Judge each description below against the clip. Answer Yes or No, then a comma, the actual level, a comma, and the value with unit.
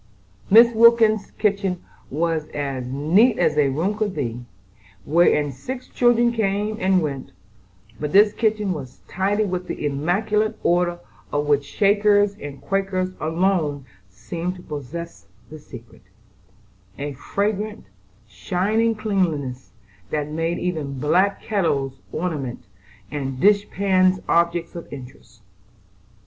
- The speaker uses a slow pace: Yes, slow, 120 wpm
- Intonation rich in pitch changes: Yes, wide, 6.1 semitones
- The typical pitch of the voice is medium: Yes, medium, 170 Hz